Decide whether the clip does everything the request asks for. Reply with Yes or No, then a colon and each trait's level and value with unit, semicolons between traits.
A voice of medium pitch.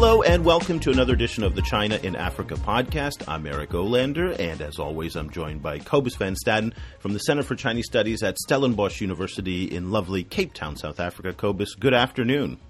No: low, 100 Hz